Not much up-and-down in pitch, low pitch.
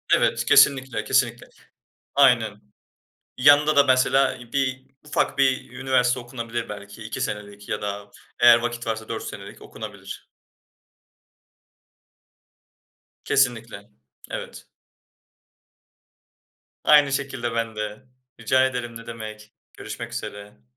No: average, 3.4 semitones; low, 120 Hz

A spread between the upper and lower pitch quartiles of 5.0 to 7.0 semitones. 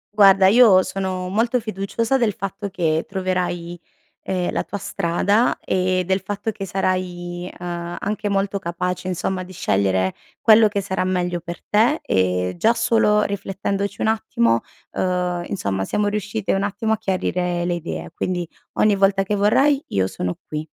No: average, 2.7 semitones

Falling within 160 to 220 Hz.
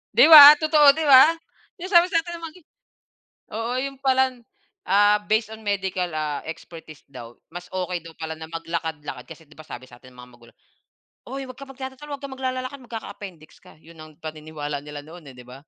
Yes: high, 190 Hz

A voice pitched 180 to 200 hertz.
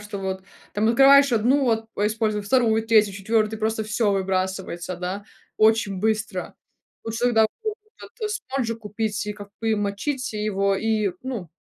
No: high, 215 Hz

